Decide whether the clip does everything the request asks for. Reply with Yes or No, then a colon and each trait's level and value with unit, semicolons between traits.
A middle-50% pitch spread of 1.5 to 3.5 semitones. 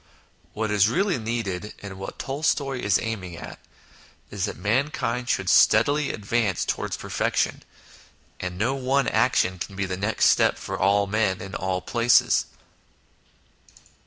No: average, 4.2 semitones